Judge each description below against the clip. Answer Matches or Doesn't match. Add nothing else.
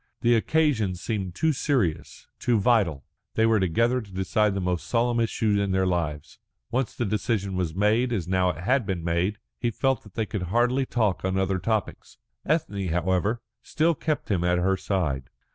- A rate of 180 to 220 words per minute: Matches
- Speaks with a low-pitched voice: Matches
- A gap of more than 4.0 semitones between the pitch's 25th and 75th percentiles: Matches